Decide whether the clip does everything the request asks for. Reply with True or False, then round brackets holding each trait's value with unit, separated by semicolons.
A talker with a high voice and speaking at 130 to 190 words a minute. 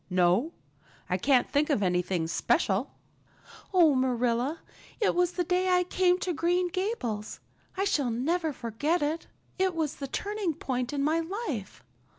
True (300 Hz; 155 wpm)